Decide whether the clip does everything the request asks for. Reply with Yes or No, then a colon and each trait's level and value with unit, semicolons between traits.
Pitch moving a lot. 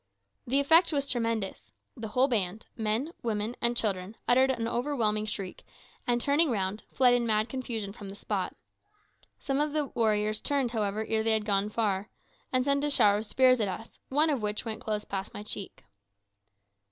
No: average, 3.7 semitones